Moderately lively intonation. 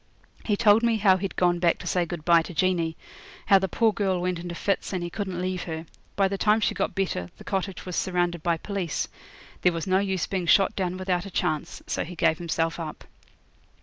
No: narrow, 2.3 semitones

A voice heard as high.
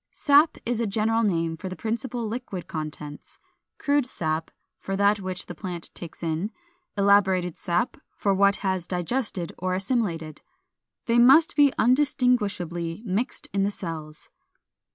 Yes: high, 195 Hz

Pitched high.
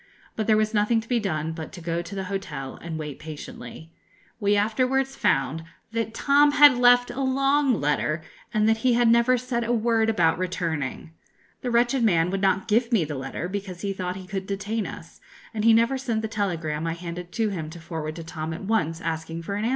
Yes: high, 200 Hz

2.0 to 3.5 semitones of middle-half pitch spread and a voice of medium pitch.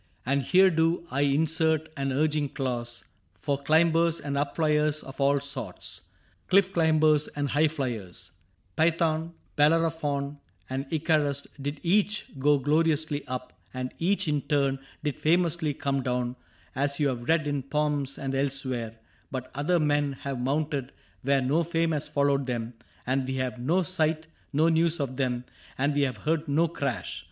Yes: average, 2.8 semitones; medium, 145 Hz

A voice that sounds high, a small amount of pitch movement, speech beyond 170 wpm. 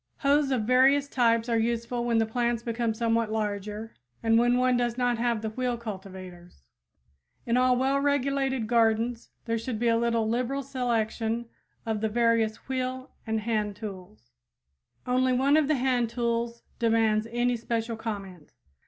No: high, 235 Hz; narrow, 2.1 semitones; average, 160 wpm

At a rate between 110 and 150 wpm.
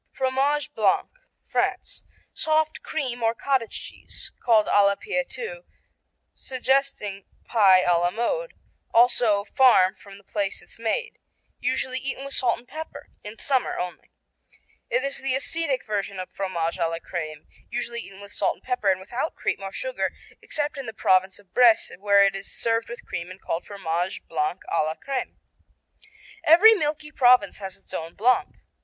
No: average, 170 wpm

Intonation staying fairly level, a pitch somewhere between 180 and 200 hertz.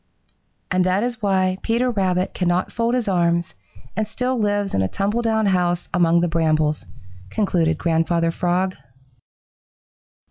No: average, 3.6 semitones; medium, 185 Hz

